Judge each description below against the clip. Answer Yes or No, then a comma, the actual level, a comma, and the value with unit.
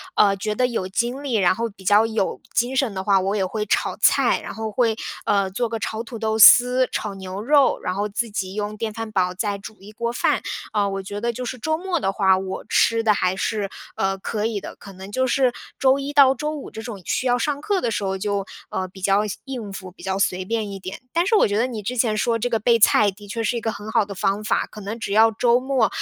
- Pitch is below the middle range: No, high, 215 Hz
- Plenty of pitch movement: No, average, 3.3 semitones